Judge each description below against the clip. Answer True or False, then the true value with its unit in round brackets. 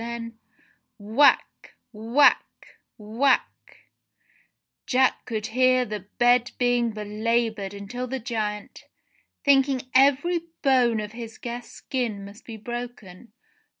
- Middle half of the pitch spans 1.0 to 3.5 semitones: True (2.9 semitones)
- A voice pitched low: False (235 Hz)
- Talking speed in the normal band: False (110 wpm)